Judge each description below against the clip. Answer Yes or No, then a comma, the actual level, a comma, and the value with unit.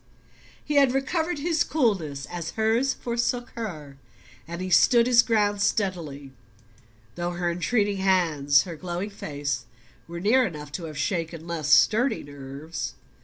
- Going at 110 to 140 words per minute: Yes, slow, 135 wpm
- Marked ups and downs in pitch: Yes, wide, 7.1 semitones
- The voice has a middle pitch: Yes, medium, 180 Hz